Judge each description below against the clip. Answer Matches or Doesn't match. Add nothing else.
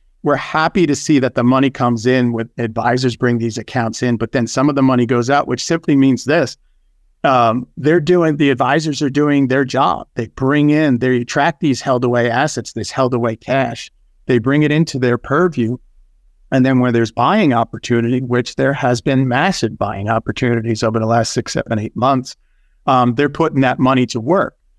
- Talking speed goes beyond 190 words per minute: Matches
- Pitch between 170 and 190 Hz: Doesn't match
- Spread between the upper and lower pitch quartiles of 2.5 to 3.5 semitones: Matches